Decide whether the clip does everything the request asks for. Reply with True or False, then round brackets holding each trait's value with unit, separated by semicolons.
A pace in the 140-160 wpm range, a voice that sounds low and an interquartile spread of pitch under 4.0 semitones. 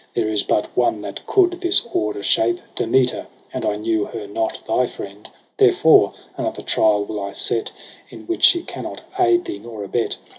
False (185 wpm; 110 Hz; 3.6 semitones)